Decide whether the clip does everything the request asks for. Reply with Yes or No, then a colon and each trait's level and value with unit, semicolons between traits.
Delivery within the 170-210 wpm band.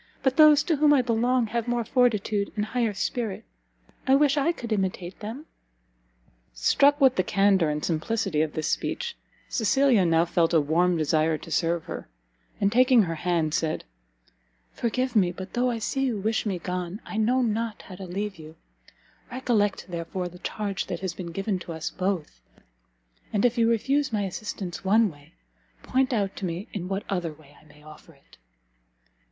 Yes: average, 180 wpm